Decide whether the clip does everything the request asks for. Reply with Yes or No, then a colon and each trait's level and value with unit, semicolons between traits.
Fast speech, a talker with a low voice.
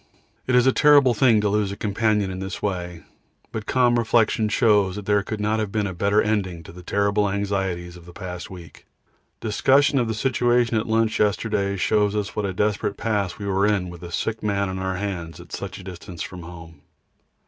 Yes: fast, 215 wpm; low, 100 Hz